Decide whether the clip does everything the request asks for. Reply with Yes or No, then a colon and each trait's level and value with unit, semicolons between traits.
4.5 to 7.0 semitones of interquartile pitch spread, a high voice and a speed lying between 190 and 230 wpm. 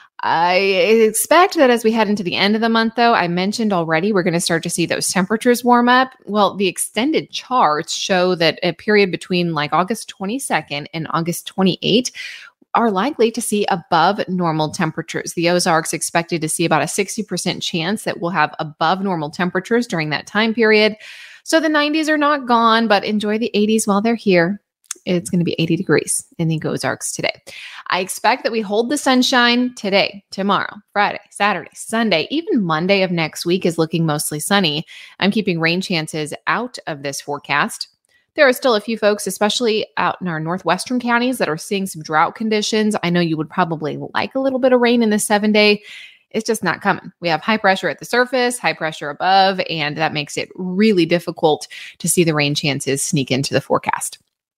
Yes: average, 5.1 semitones; high, 195 Hz; average, 200 wpm